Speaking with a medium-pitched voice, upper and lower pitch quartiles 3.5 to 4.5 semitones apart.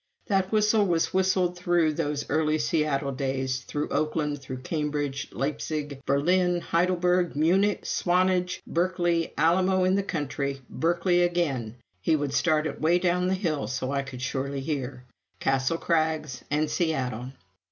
Yes: medium, 155 Hz; average, 4.2 semitones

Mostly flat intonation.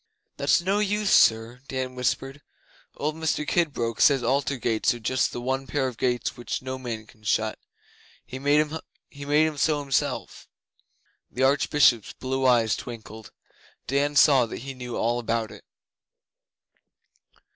No: average, 3.3 semitones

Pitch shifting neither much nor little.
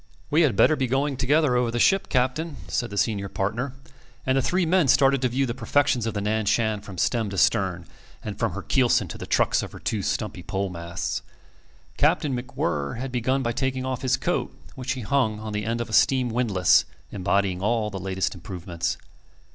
Yes: average, 4.7 semitones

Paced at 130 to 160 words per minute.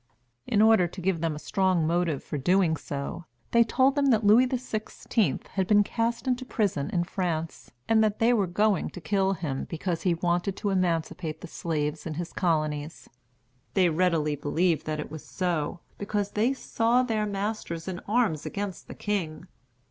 No: average, 180 wpm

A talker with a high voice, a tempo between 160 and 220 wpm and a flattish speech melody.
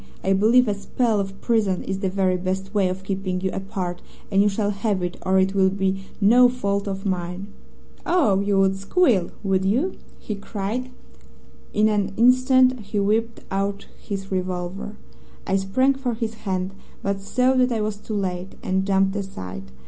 Yes: high, 195 Hz; average, 180 wpm; narrow, 2.3 semitones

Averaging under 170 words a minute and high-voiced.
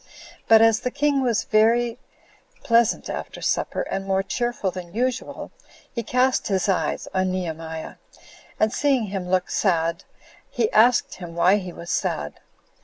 Yes: average, 150 wpm; high, 205 Hz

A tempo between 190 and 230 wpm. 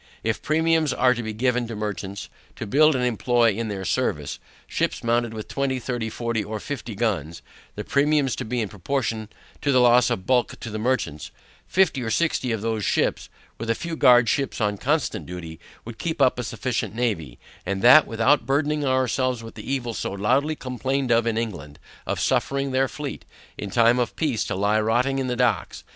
Yes: average, 200 wpm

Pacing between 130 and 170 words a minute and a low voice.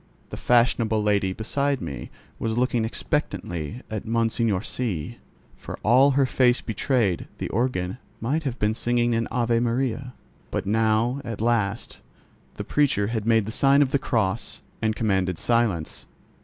Yes: average, 150 wpm; low, 115 Hz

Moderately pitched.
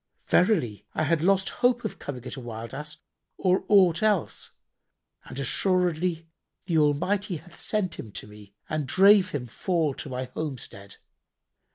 Yes: medium, 160 Hz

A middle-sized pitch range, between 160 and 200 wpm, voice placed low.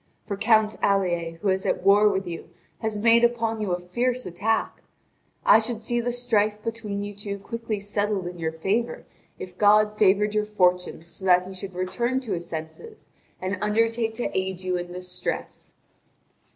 No: average, 3.5 semitones; average, 180 wpm; high, 205 Hz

